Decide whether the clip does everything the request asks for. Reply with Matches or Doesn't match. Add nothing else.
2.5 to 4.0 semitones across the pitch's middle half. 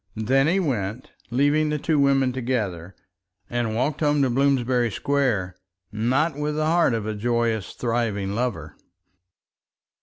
Doesn't match